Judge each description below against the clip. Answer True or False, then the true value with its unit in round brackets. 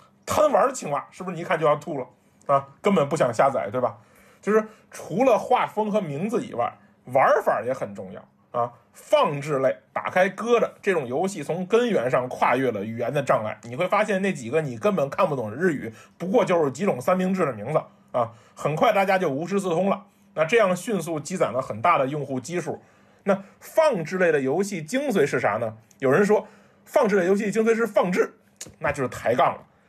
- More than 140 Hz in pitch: True (185 Hz)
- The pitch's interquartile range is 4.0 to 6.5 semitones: False (6.9 semitones)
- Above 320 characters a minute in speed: False (300 characters per minute)